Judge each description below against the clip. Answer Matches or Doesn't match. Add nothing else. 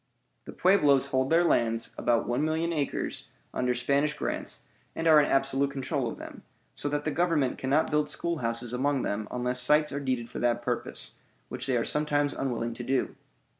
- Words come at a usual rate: Matches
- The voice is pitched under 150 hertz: Matches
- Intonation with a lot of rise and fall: Doesn't match